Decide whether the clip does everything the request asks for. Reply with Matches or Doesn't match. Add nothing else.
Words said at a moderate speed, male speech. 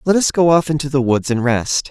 Doesn't match